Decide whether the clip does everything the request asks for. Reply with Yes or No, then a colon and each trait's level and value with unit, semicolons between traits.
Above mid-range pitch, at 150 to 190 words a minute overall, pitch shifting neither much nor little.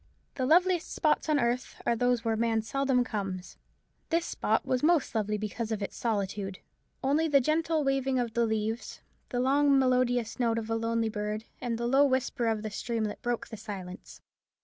Yes: high, 235 Hz; average, 185 wpm; average, 3.6 semitones